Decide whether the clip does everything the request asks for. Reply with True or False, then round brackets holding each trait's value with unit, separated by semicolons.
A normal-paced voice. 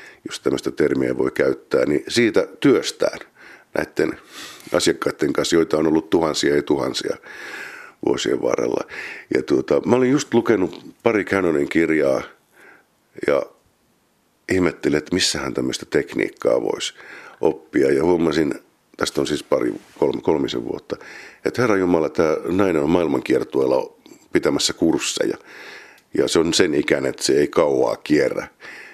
True (135 wpm)